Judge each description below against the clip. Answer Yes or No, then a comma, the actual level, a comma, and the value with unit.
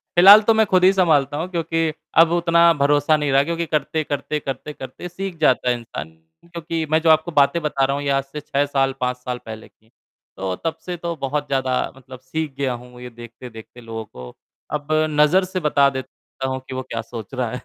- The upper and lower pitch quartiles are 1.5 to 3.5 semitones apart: No, average, 4.3 semitones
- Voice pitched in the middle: Yes, medium, 145 Hz